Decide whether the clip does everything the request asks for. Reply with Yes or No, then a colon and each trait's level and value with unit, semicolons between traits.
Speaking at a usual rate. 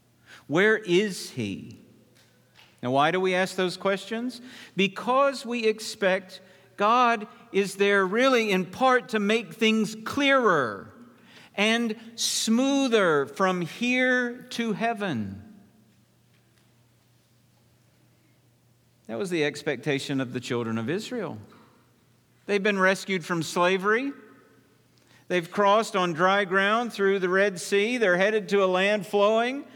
No: slow, 115 wpm